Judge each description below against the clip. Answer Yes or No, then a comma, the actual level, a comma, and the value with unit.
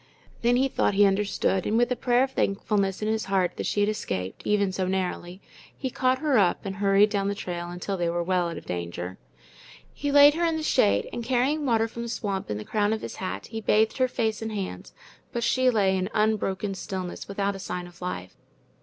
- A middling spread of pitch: Yes, average, 4.1 semitones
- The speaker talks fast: Yes, fast, 230 wpm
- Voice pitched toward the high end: Yes, high, 200 Hz